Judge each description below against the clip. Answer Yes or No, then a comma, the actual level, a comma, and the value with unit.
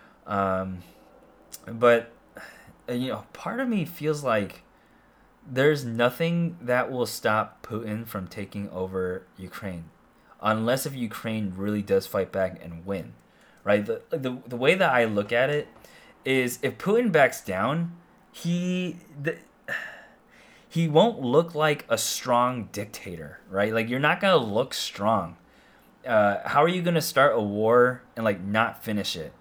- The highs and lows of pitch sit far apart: Yes, wide, 7.1 semitones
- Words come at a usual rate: Yes, average, 145 wpm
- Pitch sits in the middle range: No, low, 120 Hz